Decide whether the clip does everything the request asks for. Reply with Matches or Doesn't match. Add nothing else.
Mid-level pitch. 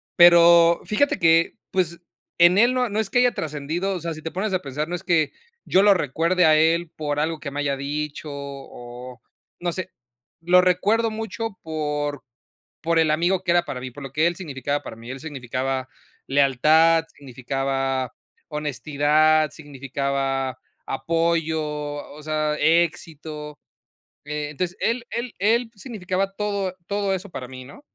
Matches